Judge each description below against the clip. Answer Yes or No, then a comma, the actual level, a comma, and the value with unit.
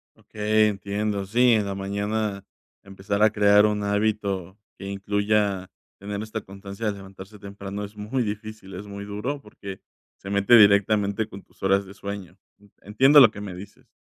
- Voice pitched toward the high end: No, low, 100 Hz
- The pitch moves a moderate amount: No, narrow, 1.3 semitones